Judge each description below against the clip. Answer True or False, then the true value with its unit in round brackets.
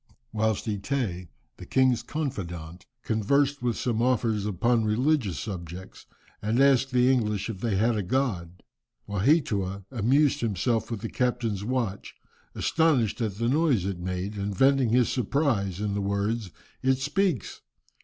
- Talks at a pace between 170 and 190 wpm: False (145 wpm)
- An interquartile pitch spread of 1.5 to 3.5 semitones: False (4.7 semitones)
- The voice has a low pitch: True (110 Hz)